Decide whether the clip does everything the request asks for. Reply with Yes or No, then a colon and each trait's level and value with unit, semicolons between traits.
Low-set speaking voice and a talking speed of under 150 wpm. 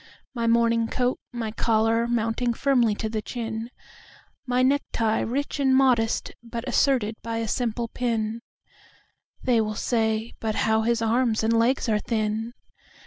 No: high, 230 Hz; average, 140 wpm